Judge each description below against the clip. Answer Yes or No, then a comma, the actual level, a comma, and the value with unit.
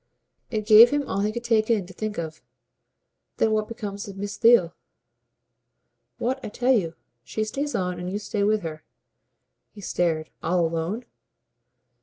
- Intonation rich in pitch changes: No, average, 4.2 semitones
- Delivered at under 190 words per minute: Yes, average, 165 wpm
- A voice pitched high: Yes, high, 210 Hz